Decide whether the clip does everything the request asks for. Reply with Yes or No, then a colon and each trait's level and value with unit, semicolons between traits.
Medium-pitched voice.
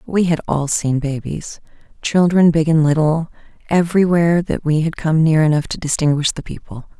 Yes: medium, 160 Hz